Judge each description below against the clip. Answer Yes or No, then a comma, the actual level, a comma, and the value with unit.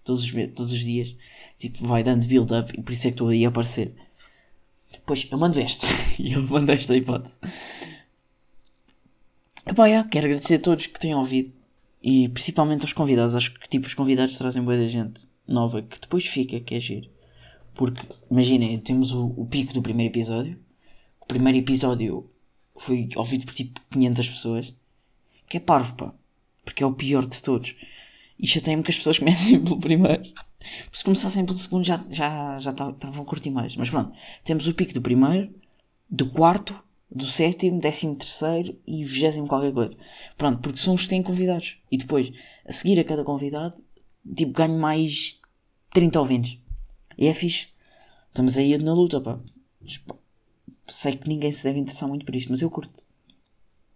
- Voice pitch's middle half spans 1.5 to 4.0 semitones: No, average, 4.5 semitones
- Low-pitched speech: Yes, low, 130 Hz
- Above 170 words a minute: Yes, average, 180 wpm